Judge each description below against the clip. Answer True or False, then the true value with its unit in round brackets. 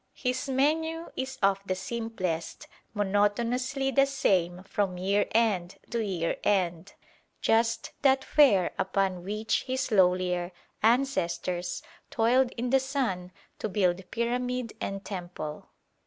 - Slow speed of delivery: True (120 wpm)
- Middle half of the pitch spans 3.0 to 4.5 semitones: False (5.5 semitones)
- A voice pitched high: True (210 Hz)